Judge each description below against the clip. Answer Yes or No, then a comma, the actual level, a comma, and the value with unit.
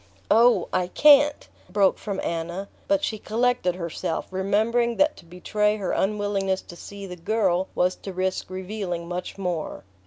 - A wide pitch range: No, average, 3.2 semitones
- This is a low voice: No, high, 195 Hz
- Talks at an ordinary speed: Yes, average, 160 wpm